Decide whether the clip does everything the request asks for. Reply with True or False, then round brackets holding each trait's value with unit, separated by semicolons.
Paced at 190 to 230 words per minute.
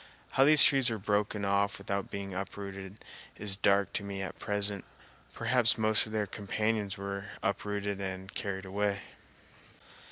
False (155 wpm)